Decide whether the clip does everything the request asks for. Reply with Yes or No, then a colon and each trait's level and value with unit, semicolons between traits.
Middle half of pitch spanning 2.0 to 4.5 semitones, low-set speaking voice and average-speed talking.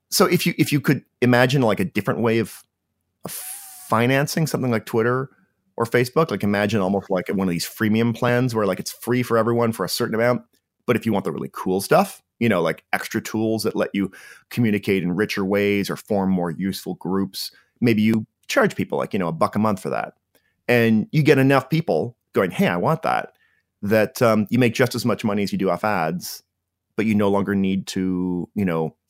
No: average, 3.9 semitones; low, 110 Hz; fast, 220 wpm